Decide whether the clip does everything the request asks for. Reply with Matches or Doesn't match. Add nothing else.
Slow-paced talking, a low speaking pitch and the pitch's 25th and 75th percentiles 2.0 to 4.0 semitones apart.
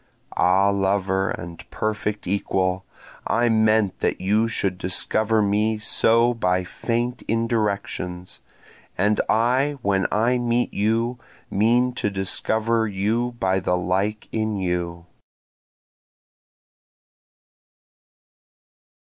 Matches